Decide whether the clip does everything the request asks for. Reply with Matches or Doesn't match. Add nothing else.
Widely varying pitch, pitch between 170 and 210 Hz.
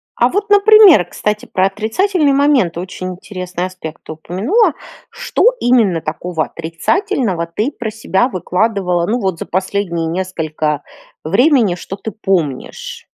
Matches